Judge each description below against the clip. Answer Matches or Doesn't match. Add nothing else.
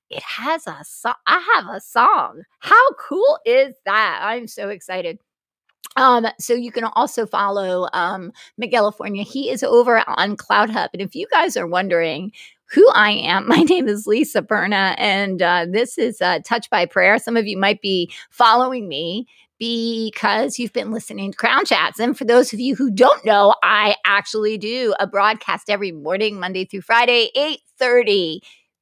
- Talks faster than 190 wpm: Doesn't match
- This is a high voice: Matches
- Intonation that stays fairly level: Doesn't match